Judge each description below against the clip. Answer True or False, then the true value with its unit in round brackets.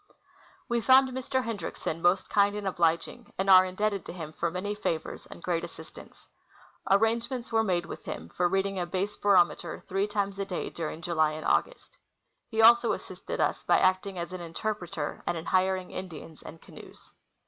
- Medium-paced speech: True (180 wpm)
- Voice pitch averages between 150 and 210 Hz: True (190 Hz)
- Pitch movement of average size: True (3.2 semitones)